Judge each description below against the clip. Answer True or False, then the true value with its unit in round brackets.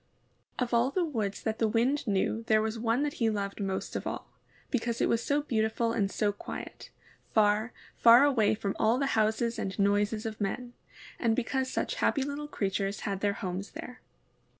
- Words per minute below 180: False (185 wpm)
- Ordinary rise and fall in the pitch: True (3.3 semitones)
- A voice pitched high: True (225 Hz)